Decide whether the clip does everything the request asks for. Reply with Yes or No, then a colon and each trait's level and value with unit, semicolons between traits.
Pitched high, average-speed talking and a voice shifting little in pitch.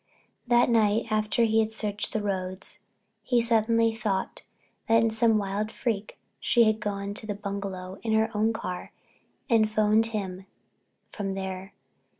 Yes: high, 215 Hz; average, 150 wpm; narrow, 2.1 semitones